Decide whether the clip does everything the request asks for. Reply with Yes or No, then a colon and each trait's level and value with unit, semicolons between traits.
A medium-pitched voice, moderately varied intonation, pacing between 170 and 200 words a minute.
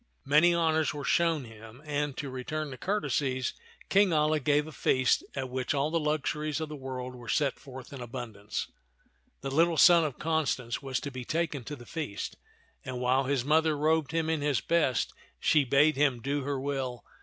Yes: medium, 145 Hz; average, 3.2 semitones; average, 195 wpm